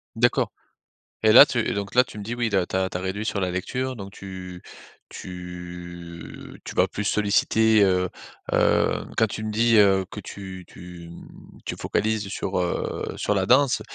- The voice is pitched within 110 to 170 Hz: No, low, 100 Hz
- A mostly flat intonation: No, average, 3.2 semitones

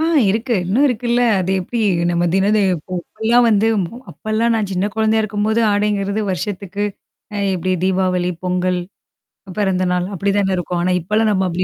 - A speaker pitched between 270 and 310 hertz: No, high, 200 Hz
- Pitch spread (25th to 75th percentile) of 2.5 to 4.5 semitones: Yes, average, 3.1 semitones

